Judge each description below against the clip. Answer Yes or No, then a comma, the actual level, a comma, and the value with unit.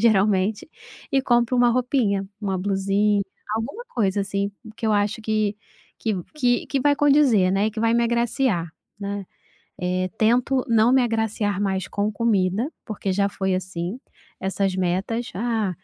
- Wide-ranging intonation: No, average, 3.5 semitones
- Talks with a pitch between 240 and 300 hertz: No, high, 210 Hz